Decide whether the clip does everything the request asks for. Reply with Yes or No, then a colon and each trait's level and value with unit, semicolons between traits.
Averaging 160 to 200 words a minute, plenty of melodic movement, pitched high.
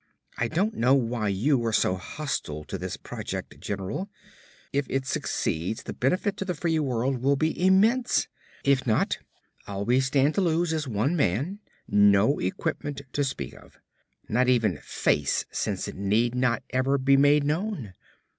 No: average, 165 wpm; wide, 5.7 semitones; low, 135 Hz